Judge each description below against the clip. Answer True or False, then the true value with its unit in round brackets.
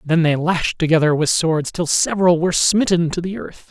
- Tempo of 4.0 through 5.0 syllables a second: False (5.3 syllables/s)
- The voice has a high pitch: False (165 Hz)